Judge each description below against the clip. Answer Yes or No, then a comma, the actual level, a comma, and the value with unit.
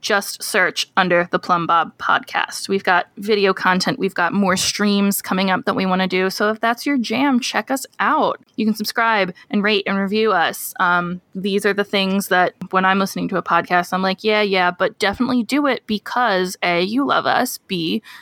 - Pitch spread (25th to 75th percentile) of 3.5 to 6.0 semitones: No, average, 2.8 semitones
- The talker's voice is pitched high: Yes, high, 195 Hz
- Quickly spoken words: Yes, fast, 210 wpm